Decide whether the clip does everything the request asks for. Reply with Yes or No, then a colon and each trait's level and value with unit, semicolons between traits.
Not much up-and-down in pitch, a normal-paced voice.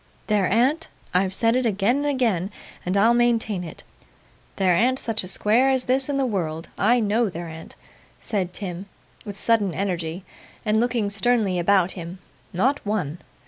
No: average, 4.7 semitones; average, 170 wpm